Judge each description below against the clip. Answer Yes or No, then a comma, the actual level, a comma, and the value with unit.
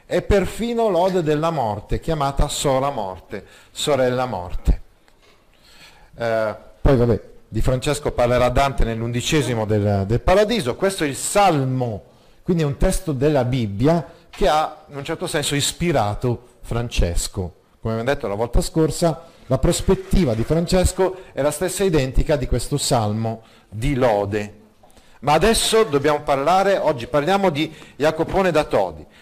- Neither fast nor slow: Yes, average, 140 wpm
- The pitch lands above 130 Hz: Yes, medium, 140 Hz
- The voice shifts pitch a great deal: Yes, wide, 6.3 semitones